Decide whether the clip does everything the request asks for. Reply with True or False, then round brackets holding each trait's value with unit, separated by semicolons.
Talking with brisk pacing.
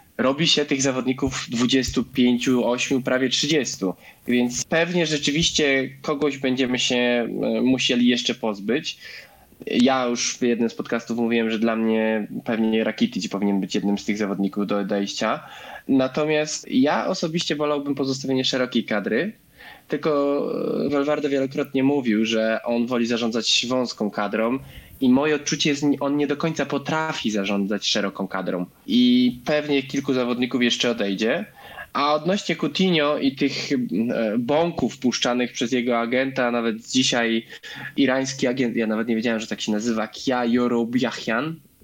False (140 wpm)